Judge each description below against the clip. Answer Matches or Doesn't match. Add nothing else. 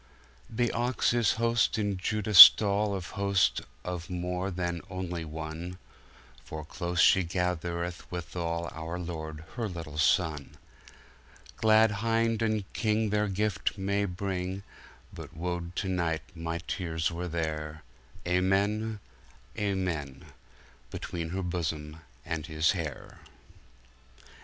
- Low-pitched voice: Matches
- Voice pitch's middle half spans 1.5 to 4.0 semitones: Matches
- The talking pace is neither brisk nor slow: Doesn't match